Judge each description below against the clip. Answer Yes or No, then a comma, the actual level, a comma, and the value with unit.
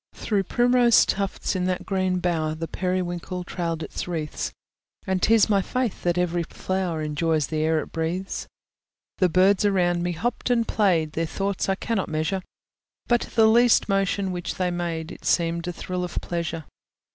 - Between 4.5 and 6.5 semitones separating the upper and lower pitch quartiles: No, average, 2.8 semitones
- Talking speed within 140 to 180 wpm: Yes, average, 170 wpm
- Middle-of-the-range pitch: Yes, medium, 180 Hz